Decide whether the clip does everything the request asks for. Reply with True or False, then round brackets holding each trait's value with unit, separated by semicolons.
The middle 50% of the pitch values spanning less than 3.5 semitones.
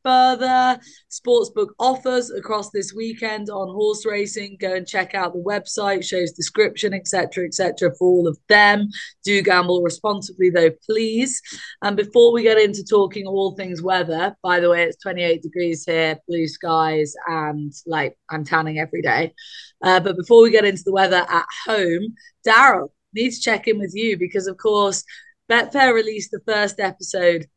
False (3.9 semitones)